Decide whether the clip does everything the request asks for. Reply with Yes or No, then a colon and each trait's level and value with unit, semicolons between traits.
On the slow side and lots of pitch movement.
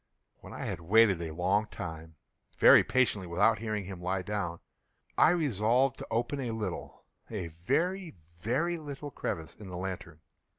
No: average, 155 wpm; wide, 6.1 semitones